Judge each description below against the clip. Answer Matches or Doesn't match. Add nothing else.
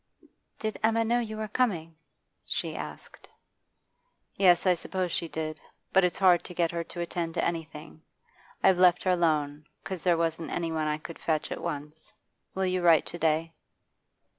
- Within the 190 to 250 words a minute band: Doesn't match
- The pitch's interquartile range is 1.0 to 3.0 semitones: Matches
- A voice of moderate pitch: Matches